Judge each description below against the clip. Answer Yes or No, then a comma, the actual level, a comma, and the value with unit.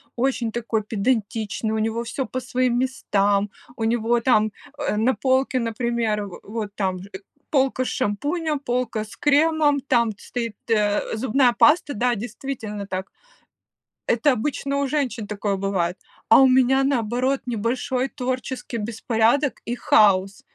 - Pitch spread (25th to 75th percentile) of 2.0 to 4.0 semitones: Yes, average, 3.6 semitones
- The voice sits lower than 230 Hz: No, high, 235 Hz